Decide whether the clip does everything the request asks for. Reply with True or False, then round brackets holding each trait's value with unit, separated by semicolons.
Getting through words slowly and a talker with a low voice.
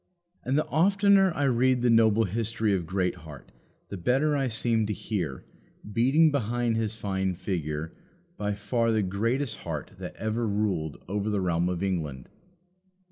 False (155 wpm; 110 Hz)